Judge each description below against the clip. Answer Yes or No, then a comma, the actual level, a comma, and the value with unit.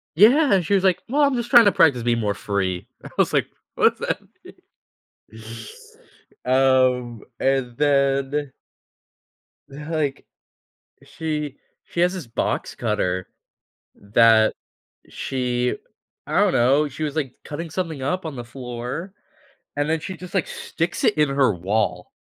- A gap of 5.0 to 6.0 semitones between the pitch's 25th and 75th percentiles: Yes, average, 5.3 semitones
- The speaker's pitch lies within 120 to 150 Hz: Yes, medium, 140 Hz